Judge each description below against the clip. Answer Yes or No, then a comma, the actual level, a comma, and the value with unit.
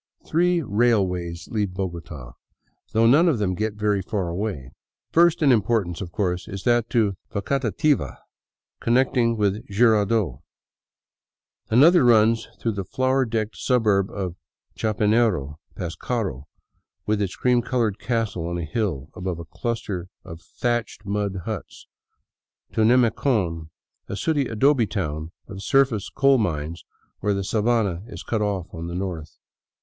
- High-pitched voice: No, low, 105 Hz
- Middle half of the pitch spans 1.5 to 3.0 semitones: No, average, 4.6 semitones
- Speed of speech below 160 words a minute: Yes, average, 140 wpm